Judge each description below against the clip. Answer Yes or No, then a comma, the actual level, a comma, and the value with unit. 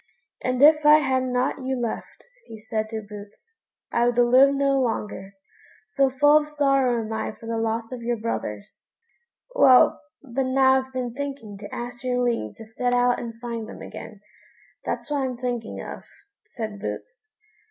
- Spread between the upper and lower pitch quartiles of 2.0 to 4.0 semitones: Yes, average, 2.9 semitones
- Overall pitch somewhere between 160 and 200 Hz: No, high, 245 Hz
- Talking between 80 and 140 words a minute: No, average, 175 wpm